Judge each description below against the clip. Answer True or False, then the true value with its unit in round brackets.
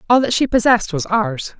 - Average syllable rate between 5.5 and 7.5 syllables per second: True (5.8 syllables/s)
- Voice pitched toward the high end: True (225 Hz)